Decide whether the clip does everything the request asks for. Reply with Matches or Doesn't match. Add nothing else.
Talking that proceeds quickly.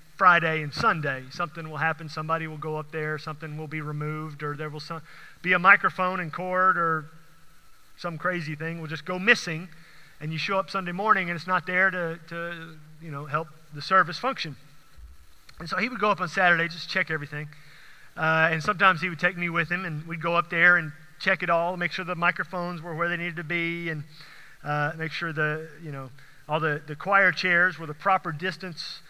Matches